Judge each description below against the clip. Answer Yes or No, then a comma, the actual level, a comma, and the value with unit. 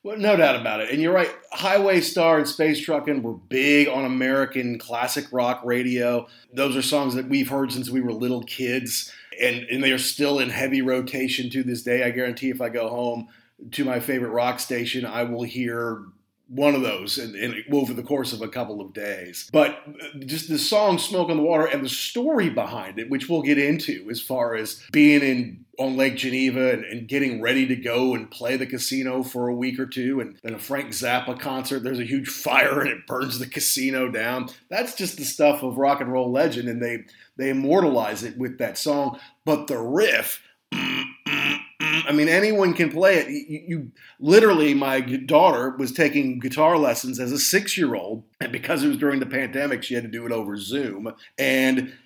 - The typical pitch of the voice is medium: No, low, 130 Hz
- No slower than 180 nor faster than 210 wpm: Yes, fast, 205 wpm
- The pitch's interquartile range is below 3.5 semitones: Yes, average, 2.8 semitones